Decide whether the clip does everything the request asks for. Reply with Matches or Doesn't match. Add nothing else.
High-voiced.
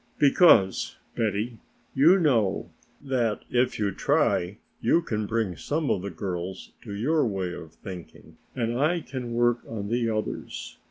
Doesn't match